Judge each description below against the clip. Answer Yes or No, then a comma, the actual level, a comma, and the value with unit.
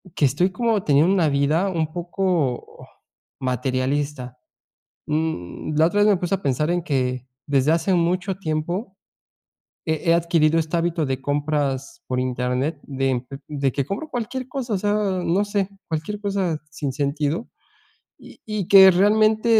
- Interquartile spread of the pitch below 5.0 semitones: No, wide, 5.6 semitones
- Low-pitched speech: No, medium, 160 Hz